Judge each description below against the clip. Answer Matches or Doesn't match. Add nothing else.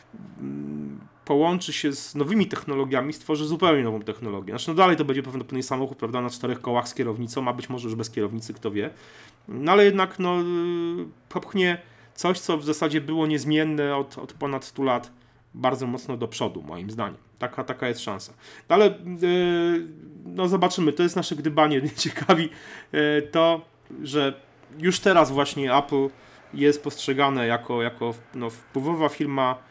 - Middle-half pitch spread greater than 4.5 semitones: Matches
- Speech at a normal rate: Doesn't match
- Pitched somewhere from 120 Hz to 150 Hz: Matches